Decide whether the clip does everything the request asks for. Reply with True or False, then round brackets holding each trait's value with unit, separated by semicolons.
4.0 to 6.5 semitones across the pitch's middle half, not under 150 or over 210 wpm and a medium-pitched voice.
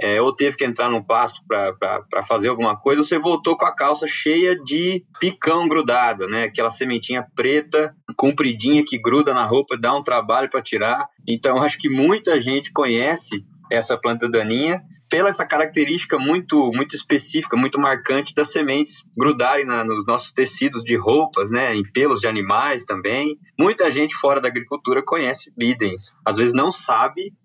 True (4.6 semitones; 170 wpm; 145 Hz)